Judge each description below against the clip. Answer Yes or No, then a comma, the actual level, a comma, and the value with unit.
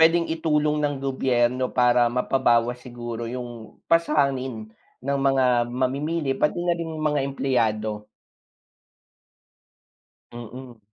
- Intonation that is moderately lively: Yes, average, 3.5 semitones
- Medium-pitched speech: No, low, 130 Hz